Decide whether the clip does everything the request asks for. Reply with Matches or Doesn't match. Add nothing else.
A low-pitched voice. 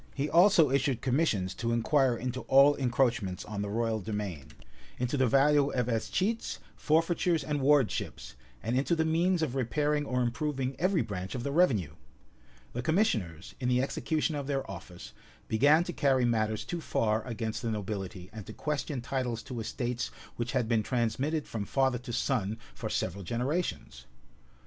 Matches